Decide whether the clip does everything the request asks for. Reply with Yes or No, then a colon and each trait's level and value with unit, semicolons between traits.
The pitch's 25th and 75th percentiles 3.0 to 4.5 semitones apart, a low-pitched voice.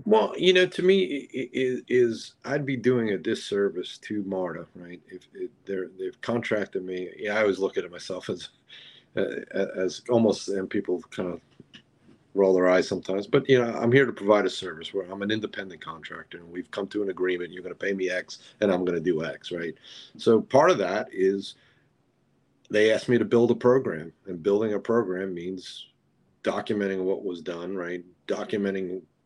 No: average, 5.0 semitones; low, 100 Hz